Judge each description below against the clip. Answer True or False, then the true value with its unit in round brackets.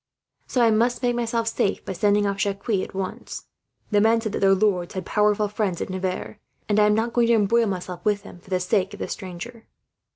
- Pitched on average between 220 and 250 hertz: False (205 Hz)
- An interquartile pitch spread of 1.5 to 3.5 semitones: True (2.9 semitones)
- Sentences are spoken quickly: True (230 wpm)